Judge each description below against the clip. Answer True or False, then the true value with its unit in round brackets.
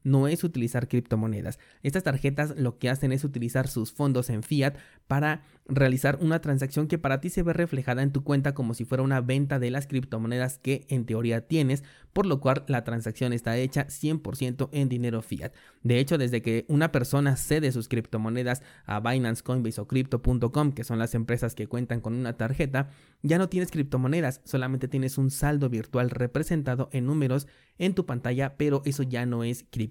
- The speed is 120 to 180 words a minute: False (190 wpm)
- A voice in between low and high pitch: False (130 Hz)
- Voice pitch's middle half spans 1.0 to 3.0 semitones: True (2.7 semitones)